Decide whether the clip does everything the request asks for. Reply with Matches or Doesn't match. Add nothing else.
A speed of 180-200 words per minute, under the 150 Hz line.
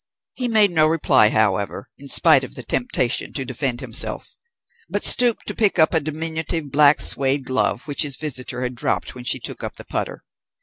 Matches